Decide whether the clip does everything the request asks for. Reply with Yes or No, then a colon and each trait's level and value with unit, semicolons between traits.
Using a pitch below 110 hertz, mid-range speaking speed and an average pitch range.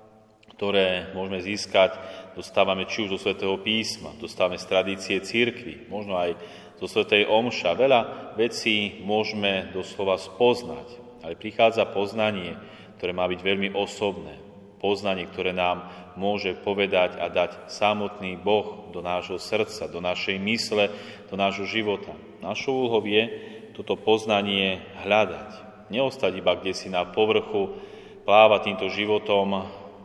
No: low, 100 Hz; average, 130 wpm; narrow, 2.0 semitones